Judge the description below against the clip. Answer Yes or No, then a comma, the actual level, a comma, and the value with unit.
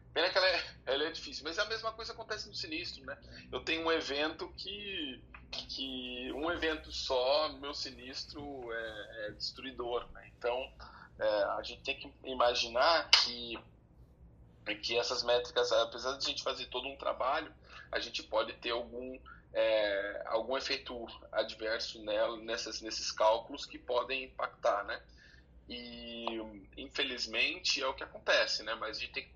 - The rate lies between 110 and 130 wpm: No, average, 165 wpm